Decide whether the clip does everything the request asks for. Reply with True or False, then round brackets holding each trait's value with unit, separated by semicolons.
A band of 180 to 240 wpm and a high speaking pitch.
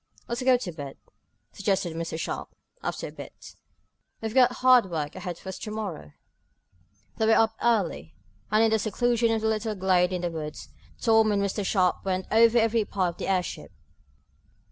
True (185 wpm; 205 Hz)